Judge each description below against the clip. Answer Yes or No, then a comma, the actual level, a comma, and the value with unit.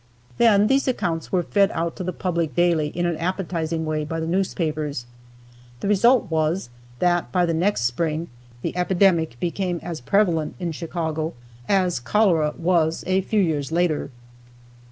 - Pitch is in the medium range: Yes, medium, 170 Hz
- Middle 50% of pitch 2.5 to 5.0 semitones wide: Yes, average, 2.8 semitones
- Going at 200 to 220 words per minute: No, average, 155 wpm